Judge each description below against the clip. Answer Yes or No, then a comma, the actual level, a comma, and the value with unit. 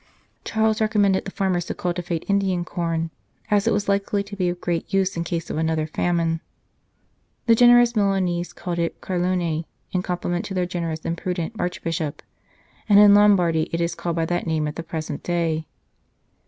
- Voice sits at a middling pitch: Yes, medium, 175 Hz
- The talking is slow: No, average, 180 wpm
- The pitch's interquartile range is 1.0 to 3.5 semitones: Yes, average, 3.0 semitones